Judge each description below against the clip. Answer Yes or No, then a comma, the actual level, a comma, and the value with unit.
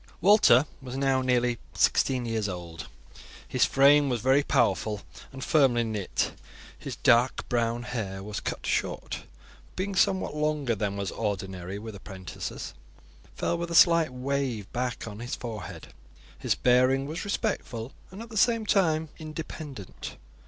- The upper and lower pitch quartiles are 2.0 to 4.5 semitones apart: No, wide, 5.5 semitones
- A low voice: Yes, low, 125 Hz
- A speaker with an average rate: Yes, average, 150 wpm